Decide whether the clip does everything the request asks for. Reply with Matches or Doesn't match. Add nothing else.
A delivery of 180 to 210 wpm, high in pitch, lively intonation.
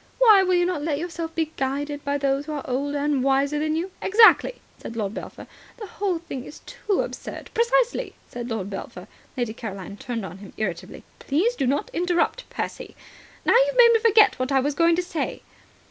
Matches